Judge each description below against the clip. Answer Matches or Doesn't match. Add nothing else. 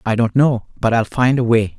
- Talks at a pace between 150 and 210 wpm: Doesn't match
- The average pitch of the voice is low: Matches